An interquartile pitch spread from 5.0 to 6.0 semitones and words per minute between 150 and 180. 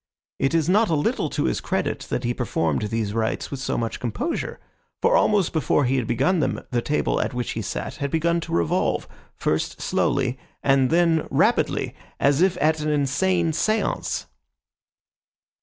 Yes: average, 5.3 semitones; average, 175 wpm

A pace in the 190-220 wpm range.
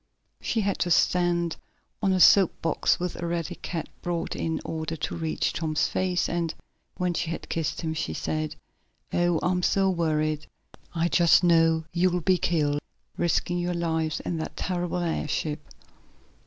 No: average, 155 wpm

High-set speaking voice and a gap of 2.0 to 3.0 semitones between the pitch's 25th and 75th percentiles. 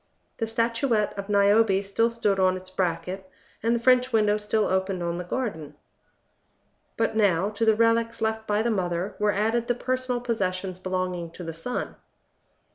No: high, 210 Hz; average, 3.6 semitones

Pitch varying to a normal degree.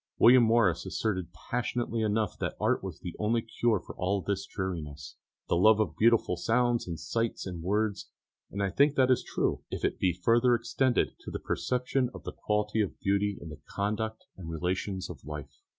Yes: average, 4.2 semitones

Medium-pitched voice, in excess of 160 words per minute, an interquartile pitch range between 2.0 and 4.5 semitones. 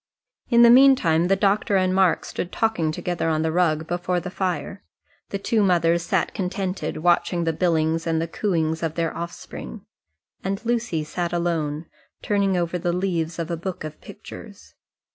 Yes: medium, 175 Hz; average, 170 wpm; average, 2.8 semitones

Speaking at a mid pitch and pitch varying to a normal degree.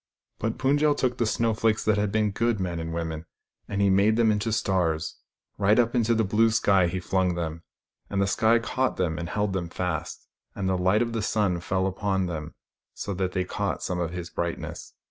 No: low, 100 Hz; average, 3.8 semitones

